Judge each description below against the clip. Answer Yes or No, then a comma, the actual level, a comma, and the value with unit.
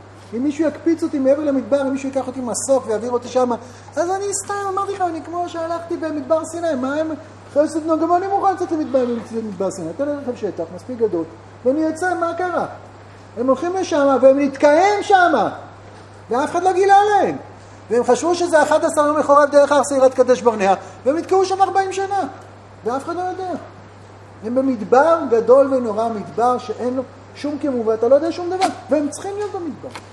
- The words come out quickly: Yes, fast, 185 wpm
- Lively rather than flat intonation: Yes, wide, 5.7 semitones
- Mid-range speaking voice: No, very high, 290 Hz